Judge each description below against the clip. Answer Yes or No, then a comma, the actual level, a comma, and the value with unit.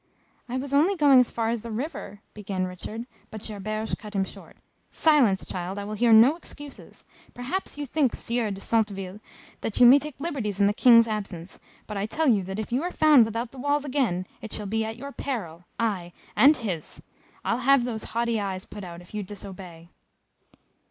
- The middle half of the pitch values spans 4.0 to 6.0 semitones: Yes, average, 4.5 semitones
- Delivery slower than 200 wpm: No, fast, 205 wpm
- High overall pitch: Yes, high, 225 Hz